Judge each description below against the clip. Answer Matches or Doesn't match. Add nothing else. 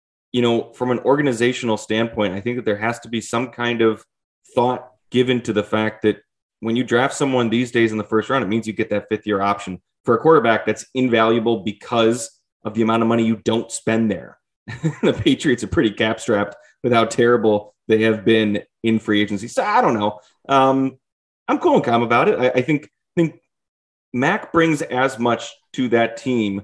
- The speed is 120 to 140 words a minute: Doesn't match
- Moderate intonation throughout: Doesn't match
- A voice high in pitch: Doesn't match